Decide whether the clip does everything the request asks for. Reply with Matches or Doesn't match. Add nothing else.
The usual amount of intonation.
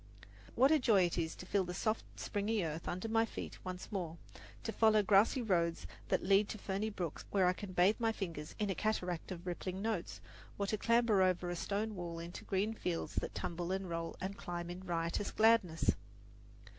Matches